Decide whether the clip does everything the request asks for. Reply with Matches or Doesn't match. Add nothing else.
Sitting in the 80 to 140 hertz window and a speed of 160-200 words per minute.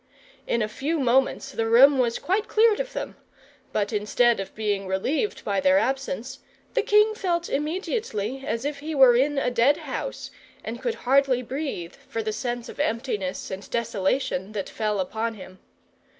Doesn't match